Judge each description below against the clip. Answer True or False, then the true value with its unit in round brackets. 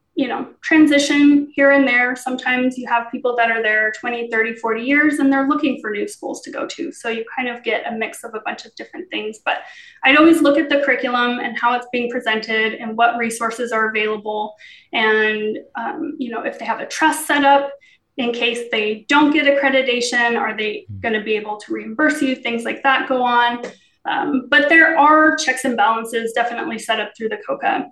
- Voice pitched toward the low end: False (245 Hz)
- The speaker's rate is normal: False (215 wpm)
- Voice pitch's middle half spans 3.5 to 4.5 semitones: True (4.0 semitones)